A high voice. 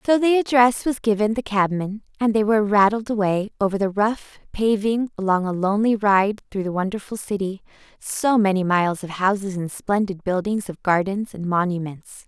Yes: high, 205 Hz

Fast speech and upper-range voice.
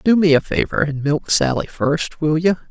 No: fast, 220 wpm; medium, 160 Hz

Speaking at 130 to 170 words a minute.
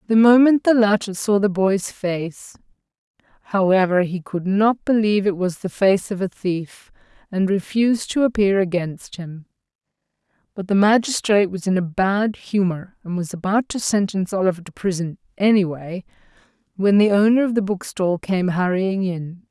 Yes: average, 165 wpm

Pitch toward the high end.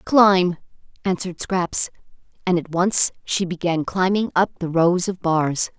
No: medium, 180 Hz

